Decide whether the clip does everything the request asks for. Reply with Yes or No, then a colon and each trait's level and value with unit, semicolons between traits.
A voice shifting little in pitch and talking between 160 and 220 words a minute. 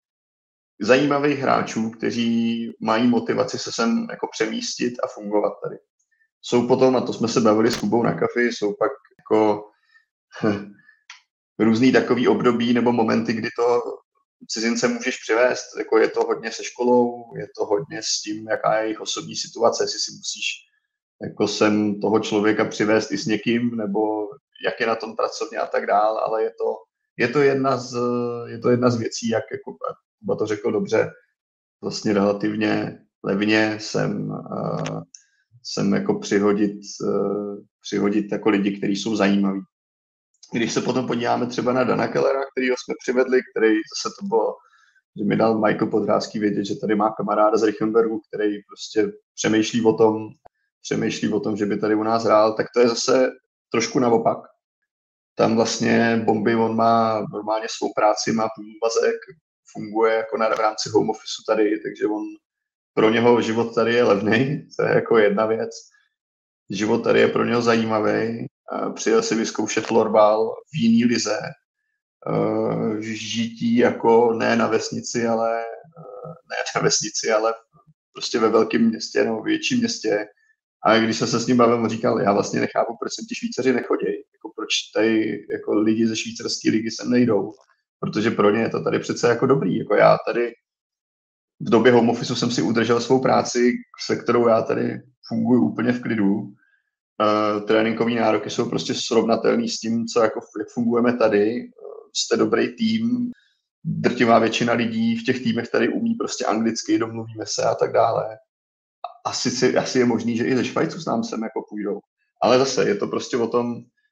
No: wide, 8.5 semitones; fast, 170 wpm